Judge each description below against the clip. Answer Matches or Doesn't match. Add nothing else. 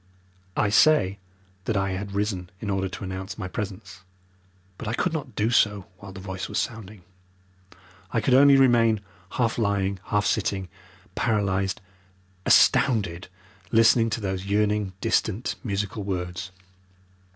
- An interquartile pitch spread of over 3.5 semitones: Doesn't match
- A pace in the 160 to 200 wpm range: Doesn't match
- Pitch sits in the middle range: Doesn't match